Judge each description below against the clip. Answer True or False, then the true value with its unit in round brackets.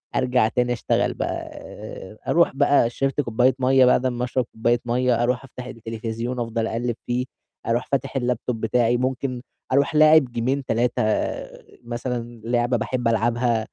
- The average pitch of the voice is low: True (120 Hz)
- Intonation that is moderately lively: False (1.6 semitones)